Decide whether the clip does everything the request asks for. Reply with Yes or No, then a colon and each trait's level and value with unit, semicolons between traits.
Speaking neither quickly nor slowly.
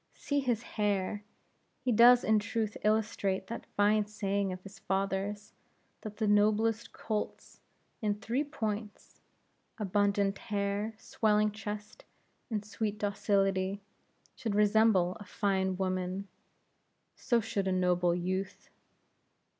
No: slow, 120 wpm